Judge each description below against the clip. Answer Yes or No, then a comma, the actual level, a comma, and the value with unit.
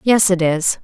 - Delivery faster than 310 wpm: No, fast, 215 wpm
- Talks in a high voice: No, medium, 180 Hz